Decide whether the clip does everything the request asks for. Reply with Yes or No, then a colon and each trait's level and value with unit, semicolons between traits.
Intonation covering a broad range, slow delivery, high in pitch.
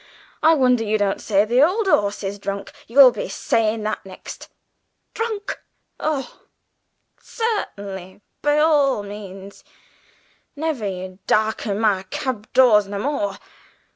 Yes: wide, 5.9 semitones; slow, 125 wpm; high, 215 Hz